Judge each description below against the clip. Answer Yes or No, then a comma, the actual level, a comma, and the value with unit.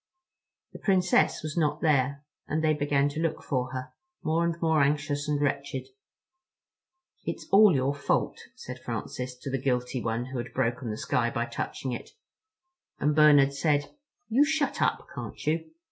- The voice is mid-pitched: Yes, medium, 145 Hz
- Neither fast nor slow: Yes, average, 165 wpm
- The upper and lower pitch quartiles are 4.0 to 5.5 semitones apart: No, average, 3.2 semitones